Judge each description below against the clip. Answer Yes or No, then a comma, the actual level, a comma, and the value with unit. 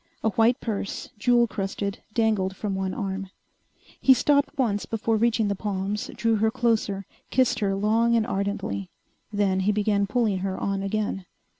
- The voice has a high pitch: Yes, high, 210 Hz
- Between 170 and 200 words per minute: No, average, 160 wpm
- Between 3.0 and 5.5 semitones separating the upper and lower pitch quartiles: No, narrow, 2.6 semitones